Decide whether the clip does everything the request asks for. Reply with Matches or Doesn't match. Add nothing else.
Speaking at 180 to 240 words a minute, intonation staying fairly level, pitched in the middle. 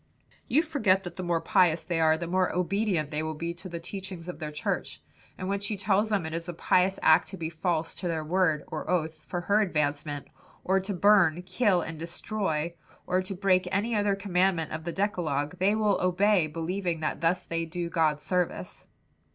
Doesn't match